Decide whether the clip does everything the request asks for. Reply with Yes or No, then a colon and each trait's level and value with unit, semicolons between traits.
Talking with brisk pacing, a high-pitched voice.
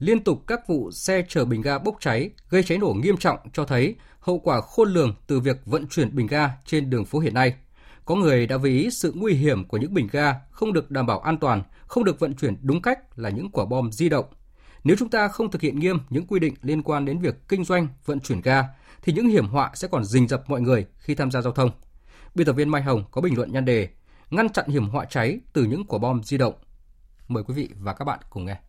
No: fast, 260 wpm; medium, 140 Hz